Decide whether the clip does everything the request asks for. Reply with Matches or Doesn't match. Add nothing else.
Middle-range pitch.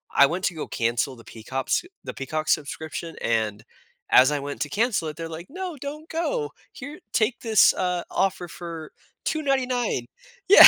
Matches